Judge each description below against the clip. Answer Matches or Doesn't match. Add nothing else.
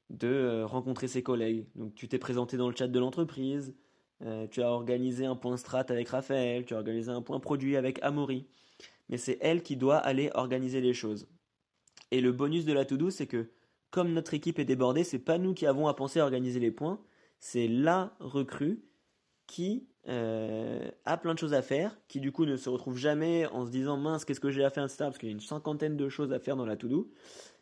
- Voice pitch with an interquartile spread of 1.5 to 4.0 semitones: Matches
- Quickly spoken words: Matches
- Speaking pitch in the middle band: Doesn't match